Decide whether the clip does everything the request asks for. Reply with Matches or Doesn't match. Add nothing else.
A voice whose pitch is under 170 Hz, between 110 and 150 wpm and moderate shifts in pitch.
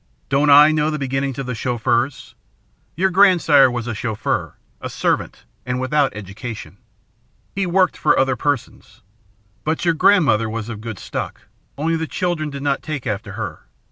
Doesn't match